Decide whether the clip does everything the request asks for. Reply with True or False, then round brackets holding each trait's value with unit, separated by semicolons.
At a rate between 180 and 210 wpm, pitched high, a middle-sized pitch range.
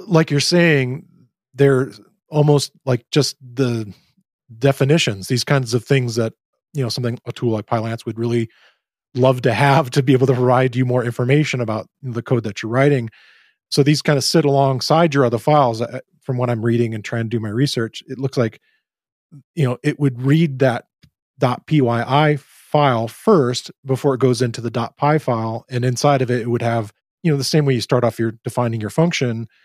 False (200 wpm; 130 Hz; 3.4 semitones)